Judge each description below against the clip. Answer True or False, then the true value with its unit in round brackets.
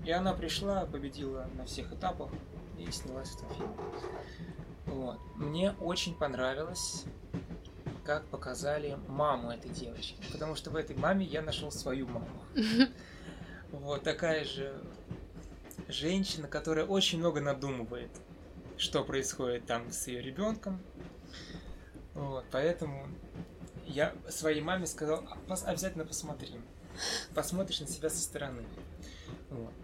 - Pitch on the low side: False (150 Hz)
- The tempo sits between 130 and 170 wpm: False (115 wpm)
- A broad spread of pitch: False (4.7 semitones)